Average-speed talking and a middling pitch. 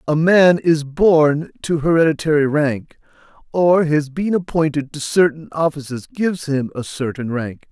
Yes: average, 150 wpm; medium, 150 Hz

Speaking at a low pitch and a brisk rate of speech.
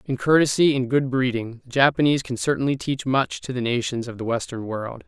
Yes: low, 130 Hz; fast, 215 wpm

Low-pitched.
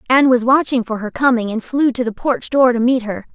No: high, 245 Hz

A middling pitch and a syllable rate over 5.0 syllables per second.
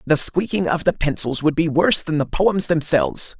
Yes: medium, 160 Hz; 5.2 syllables/s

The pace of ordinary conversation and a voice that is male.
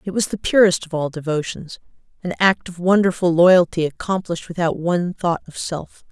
No: average, 175 wpm; female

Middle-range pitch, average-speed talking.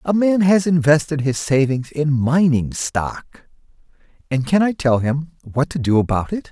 Yes: medium, 145 Hz; average, 175 wpm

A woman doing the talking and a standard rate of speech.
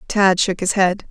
No: female; fast, 215 wpm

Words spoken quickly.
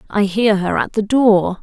Yes: fast, 220 wpm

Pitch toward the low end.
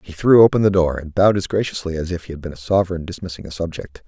Yes: very low, 90 Hz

